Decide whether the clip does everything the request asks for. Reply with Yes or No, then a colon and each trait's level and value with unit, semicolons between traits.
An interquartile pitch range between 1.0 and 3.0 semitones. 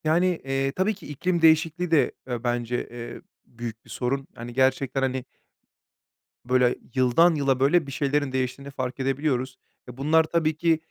No: average, 3.8 semitones